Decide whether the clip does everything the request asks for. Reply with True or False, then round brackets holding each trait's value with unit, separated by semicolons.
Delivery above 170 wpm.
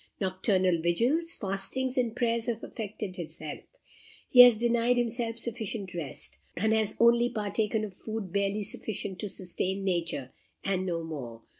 False (150 wpm)